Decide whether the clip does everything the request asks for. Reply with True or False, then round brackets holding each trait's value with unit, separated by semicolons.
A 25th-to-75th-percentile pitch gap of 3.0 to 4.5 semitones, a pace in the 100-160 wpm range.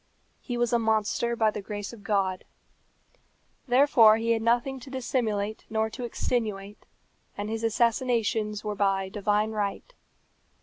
False (2.4 semitones; 140 wpm)